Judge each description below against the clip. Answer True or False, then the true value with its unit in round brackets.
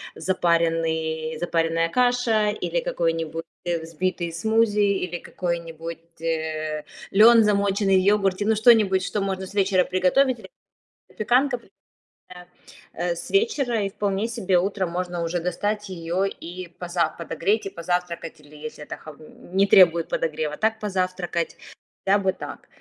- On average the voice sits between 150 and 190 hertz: True (185 Hz)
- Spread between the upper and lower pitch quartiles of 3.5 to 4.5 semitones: True (3.8 semitones)